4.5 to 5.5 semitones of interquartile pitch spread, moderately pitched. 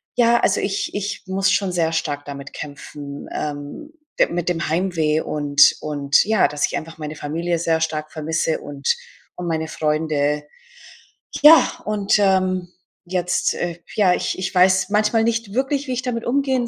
Yes: average, 5.1 semitones; medium, 175 Hz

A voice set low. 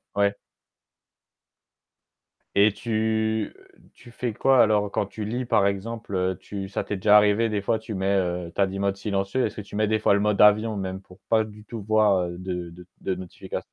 Yes: low, 105 Hz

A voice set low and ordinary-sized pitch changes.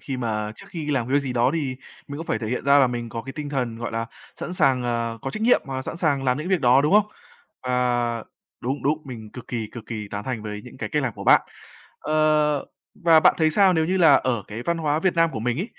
Yes: low, 130 Hz; average, 4.5 semitones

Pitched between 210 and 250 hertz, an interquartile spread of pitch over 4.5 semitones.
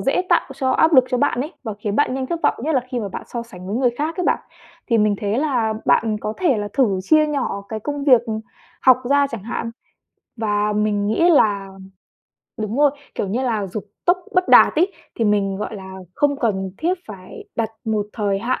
Yes: high, 230 Hz; average, 5.2 semitones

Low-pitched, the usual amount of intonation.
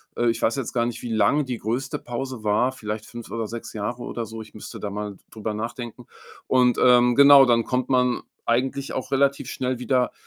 No: low, 120 Hz; narrow, 2.3 semitones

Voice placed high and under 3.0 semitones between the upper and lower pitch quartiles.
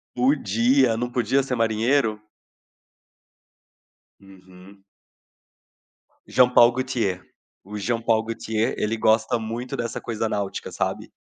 No: low, 115 Hz; narrow, 2.4 semitones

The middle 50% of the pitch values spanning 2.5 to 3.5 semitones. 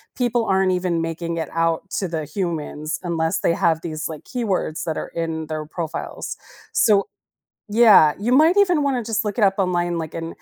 No: average, 4.4 semitones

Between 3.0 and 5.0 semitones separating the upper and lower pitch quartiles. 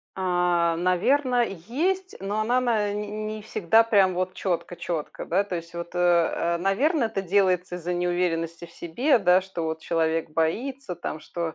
Yes: average, 4.0 semitones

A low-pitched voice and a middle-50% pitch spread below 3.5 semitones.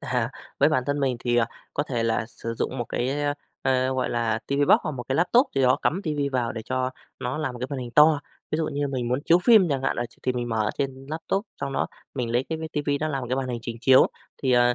Yes: low, 130 Hz; average, 3.0 semitones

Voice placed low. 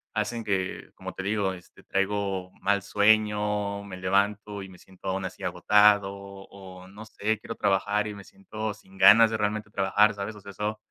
Yes: low, 100 Hz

